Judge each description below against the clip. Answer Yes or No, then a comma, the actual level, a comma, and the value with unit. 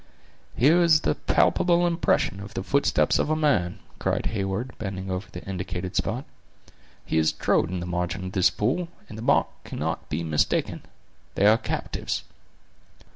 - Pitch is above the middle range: No, low, 100 Hz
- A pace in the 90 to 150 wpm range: No, average, 165 wpm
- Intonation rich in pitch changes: Yes, wide, 7.2 semitones